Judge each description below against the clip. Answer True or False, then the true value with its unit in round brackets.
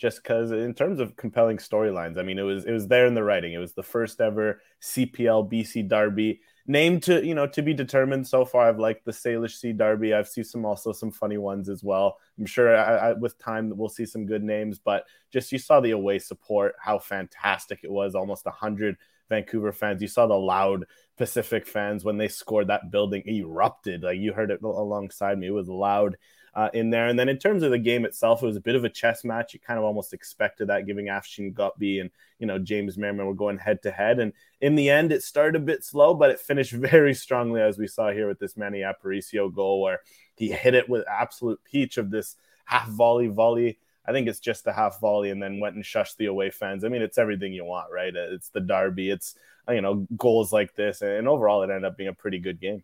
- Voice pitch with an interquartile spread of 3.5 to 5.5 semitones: False (2.7 semitones)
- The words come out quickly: True (240 wpm)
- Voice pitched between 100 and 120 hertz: True (110 Hz)